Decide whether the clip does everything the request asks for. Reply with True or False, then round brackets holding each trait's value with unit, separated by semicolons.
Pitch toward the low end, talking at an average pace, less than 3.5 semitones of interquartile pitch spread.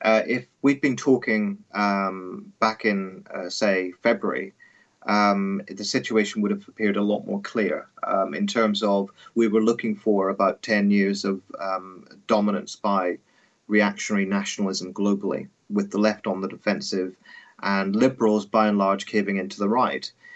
True (105 Hz; 160 wpm; 2.4 semitones)